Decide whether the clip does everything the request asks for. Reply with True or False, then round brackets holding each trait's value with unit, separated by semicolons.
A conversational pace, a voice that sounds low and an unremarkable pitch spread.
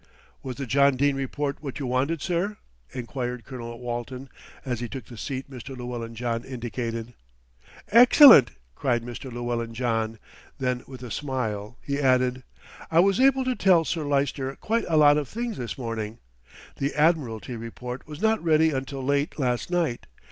True (165 wpm; 130 Hz; 3.6 semitones)